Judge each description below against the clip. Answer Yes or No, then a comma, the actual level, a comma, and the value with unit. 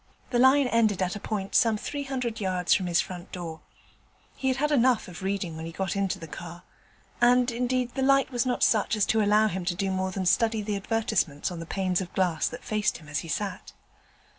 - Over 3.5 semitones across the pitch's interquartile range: Yes, average, 5.1 semitones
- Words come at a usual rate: No, fast, 230 wpm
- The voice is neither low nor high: No, high, 200 Hz